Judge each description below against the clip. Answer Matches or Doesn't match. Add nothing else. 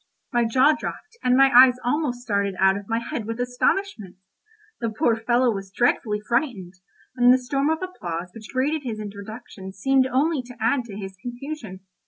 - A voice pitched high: Matches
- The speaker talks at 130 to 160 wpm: Doesn't match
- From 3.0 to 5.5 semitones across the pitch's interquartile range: Matches